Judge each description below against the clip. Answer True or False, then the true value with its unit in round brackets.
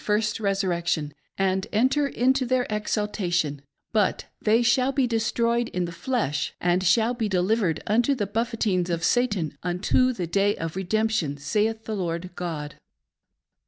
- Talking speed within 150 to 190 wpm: True (155 wpm)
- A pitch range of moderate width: True (4.8 semitones)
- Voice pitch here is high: True (210 Hz)